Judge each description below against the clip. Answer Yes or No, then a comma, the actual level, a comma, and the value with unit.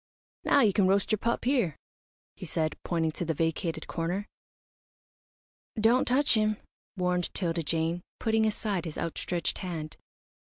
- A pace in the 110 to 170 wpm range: Yes, average, 140 wpm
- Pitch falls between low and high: Yes, medium, 180 Hz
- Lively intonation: No, average, 4.6 semitones